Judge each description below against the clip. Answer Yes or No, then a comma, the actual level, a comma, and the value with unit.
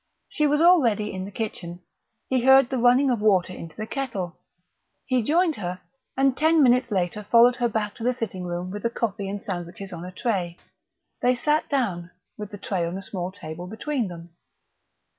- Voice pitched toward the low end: No, high, 210 Hz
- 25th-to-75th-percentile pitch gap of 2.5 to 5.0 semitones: No, wide, 5.5 semitones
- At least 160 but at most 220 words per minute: Yes, average, 195 wpm